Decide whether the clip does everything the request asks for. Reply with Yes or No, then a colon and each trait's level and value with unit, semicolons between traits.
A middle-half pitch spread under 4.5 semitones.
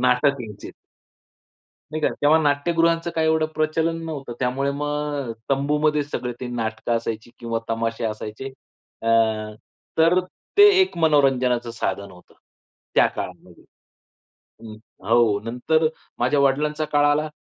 No: average, 4.8 semitones